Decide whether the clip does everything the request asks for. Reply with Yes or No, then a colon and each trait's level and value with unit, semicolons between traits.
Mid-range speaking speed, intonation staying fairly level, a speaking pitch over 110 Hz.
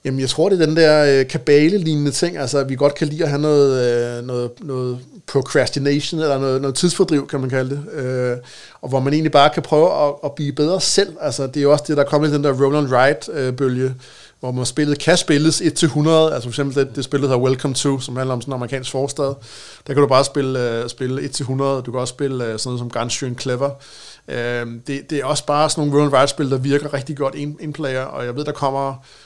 No: fast, 240 wpm; narrow, 2.3 semitones; medium, 140 Hz